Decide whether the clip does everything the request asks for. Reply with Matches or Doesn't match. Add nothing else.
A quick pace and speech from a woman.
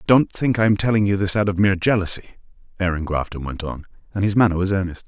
Doesn't match